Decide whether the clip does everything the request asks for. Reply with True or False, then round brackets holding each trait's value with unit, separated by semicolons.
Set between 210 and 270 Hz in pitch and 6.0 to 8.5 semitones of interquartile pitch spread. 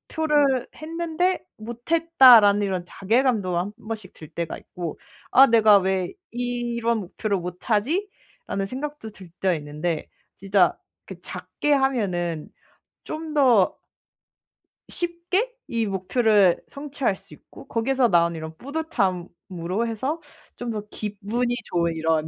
True (215 Hz; 6.6 semitones)